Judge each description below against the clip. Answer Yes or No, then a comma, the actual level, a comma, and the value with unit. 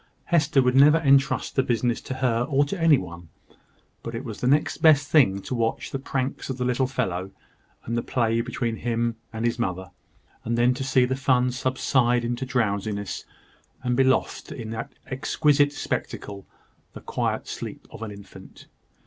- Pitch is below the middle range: Yes, low, 125 Hz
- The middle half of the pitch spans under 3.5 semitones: Yes, average, 2.8 semitones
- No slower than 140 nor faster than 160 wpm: No, average, 180 wpm